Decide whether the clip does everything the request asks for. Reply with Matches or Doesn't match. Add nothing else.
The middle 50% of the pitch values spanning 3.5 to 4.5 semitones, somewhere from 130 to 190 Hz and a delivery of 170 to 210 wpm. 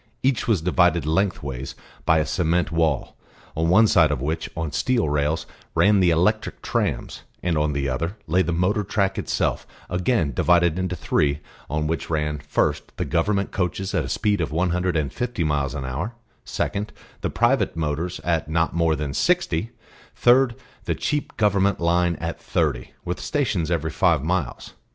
Doesn't match